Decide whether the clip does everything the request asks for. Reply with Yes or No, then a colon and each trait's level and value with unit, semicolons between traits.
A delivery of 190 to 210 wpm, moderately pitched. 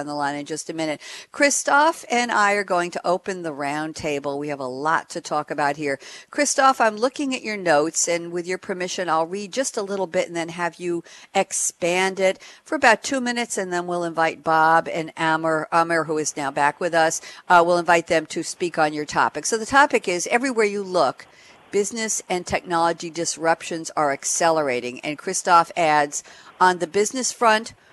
Yes: average, 200 wpm; medium, 175 Hz